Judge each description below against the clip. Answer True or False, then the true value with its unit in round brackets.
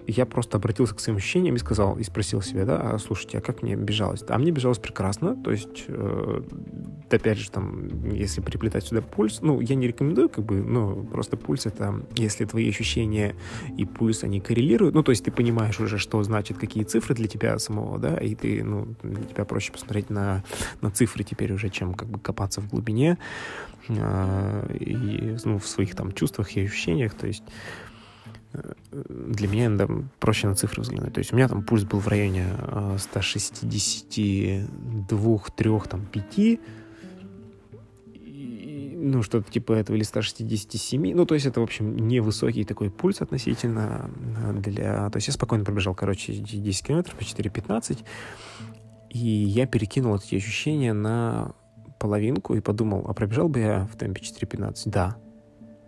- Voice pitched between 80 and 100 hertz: False (110 Hz)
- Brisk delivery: True (165 wpm)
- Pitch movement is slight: True (2.2 semitones)